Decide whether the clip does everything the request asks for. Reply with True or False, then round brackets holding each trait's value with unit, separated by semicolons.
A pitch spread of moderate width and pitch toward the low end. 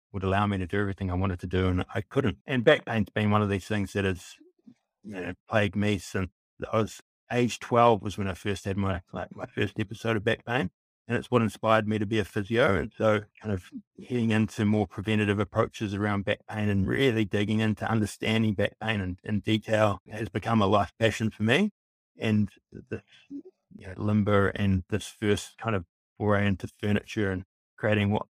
False (1.9 semitones; 105 Hz)